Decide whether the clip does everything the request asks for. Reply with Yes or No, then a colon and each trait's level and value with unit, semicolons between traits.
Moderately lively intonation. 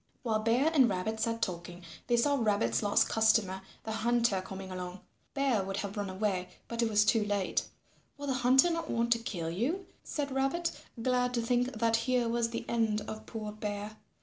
Yes: average, 3.5 semitones